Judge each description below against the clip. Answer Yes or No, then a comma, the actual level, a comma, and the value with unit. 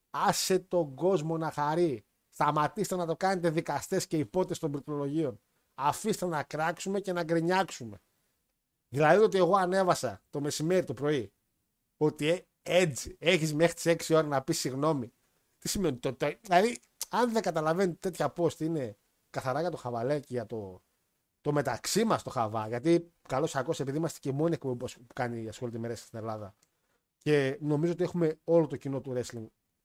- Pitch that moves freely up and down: No, average, 4.5 semitones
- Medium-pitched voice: Yes, medium, 155 Hz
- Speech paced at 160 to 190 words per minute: Yes, average, 165 wpm